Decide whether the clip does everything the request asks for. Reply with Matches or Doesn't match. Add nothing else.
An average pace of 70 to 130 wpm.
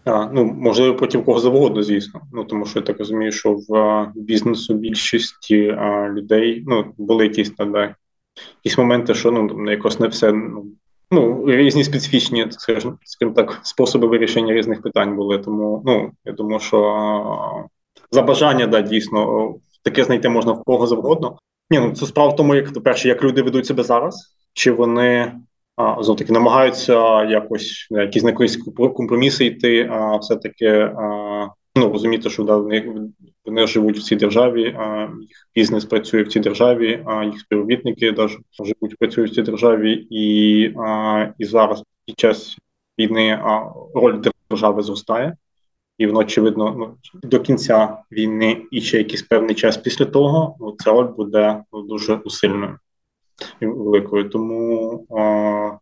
Doesn't match